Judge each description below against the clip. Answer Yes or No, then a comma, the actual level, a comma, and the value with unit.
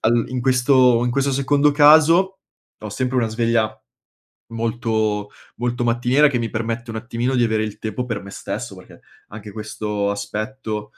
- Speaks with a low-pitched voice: Yes, low, 120 Hz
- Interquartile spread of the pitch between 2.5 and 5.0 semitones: Yes, average, 2.9 semitones